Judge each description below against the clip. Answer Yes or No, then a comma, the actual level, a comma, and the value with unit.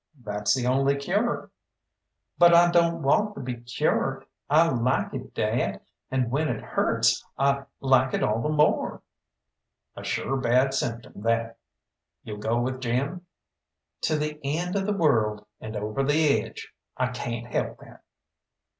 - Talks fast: No, average, 155 wpm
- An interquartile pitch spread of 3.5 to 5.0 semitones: Yes, average, 4.4 semitones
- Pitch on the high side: No, low, 135 Hz